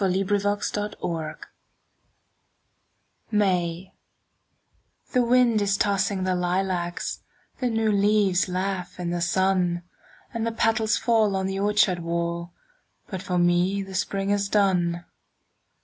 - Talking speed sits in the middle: No, slow, 115 wpm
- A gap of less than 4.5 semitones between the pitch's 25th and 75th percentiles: Yes, average, 2.7 semitones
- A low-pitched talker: No, high, 195 Hz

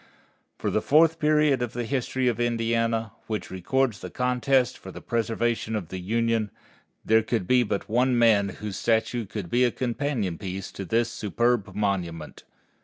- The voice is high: No, low, 115 Hz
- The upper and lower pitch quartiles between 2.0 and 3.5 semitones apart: Yes, average, 3.0 semitones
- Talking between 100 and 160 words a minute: No, average, 170 wpm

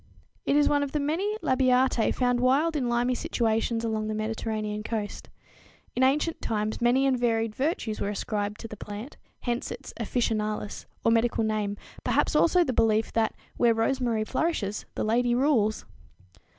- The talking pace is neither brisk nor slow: Yes, average, 165 wpm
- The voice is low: No, high, 230 Hz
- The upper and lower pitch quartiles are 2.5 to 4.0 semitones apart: Yes, average, 3.2 semitones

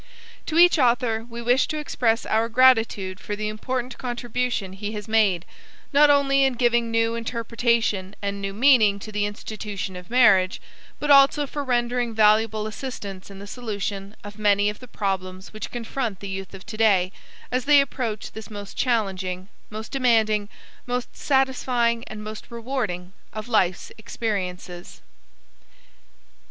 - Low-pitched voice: No, high, 220 Hz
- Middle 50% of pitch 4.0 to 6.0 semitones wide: No, average, 3.4 semitones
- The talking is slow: No, average, 150 wpm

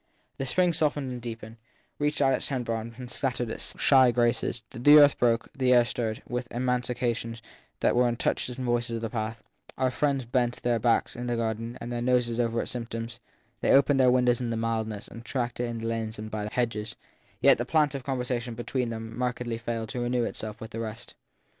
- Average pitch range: No, narrow, 1.6 semitones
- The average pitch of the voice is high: No, low, 120 Hz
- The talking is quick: Yes, fast, 215 wpm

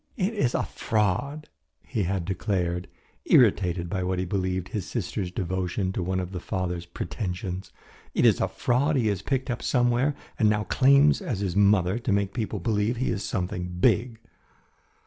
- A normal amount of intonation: Yes, average, 4.8 semitones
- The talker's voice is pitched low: Yes, low, 100 Hz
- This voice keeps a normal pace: Yes, average, 175 wpm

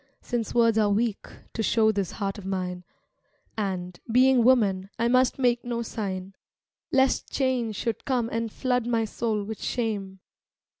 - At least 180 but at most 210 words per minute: No, average, 155 wpm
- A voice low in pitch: No, high, 225 Hz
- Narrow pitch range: No, average, 3.4 semitones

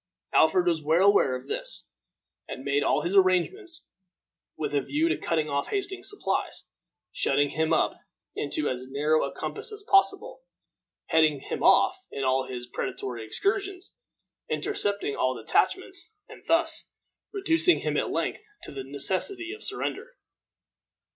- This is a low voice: No, medium, 180 Hz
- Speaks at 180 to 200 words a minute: No, average, 145 wpm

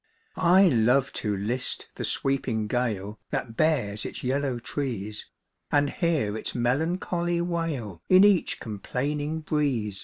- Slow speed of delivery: Yes, slow, 125 wpm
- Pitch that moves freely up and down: Yes, wide, 6.3 semitones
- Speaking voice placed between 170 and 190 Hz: No, low, 130 Hz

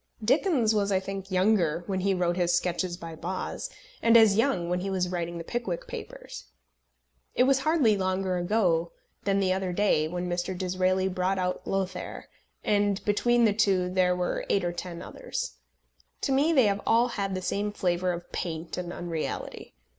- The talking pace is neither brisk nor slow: Yes, average, 180 wpm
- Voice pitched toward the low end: No, medium, 185 Hz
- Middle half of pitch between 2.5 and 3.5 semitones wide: Yes, average, 2.8 semitones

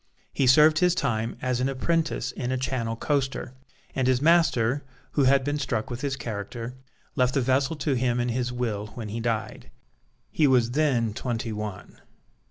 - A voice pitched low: Yes, low, 125 Hz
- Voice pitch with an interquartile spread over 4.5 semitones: No, average, 3.0 semitones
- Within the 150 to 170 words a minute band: No, average, 180 wpm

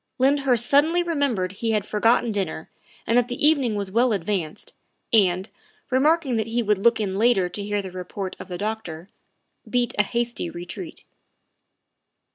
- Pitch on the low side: No, high, 220 Hz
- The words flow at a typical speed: Yes, average, 165 wpm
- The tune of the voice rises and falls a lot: No, average, 4.3 semitones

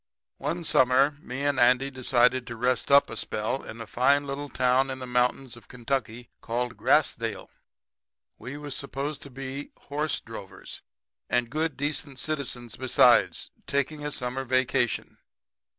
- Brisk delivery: No, average, 150 wpm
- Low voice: Yes, low, 130 Hz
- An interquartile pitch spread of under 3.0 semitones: Yes, narrow, 2.4 semitones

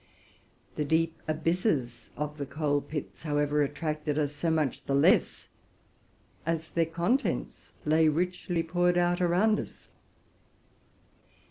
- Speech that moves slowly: Yes, slow, 120 wpm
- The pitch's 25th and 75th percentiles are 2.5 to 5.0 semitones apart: Yes, average, 2.8 semitones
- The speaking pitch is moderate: Yes, medium, 155 Hz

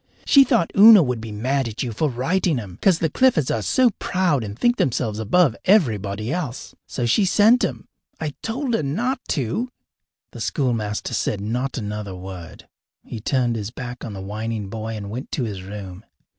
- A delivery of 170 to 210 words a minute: Yes, average, 190 wpm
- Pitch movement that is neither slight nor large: No, wide, 8.3 semitones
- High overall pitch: No, low, 125 Hz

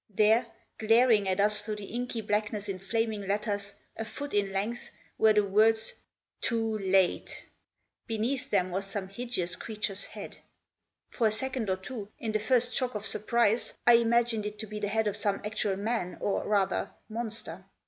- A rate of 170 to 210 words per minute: Yes, average, 175 wpm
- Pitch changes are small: Yes, narrow, 2.2 semitones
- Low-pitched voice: No, high, 215 Hz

